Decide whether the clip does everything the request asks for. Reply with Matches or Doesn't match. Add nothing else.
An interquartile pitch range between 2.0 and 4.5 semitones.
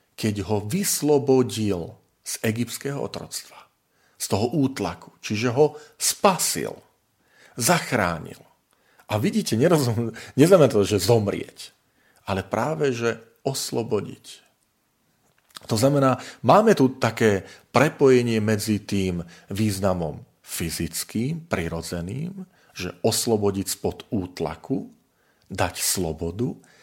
Doesn't match